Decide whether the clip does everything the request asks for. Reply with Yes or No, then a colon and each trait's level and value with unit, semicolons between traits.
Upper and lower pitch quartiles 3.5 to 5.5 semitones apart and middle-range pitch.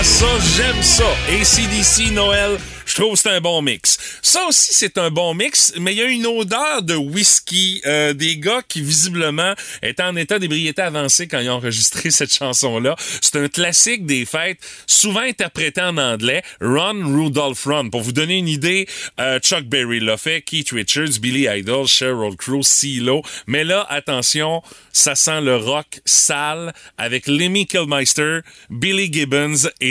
Yes: average, 4.7 semitones; medium, 155 Hz